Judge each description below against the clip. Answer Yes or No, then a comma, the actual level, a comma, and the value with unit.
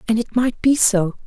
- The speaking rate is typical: No, fast, 240 wpm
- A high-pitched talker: Yes, high, 225 Hz